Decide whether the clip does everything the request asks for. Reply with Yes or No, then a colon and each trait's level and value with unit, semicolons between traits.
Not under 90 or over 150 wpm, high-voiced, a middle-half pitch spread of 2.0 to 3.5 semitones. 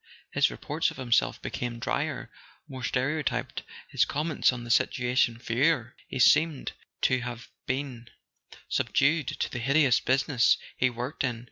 No: average, 140 wpm; low, 130 Hz; narrow, 2.6 semitones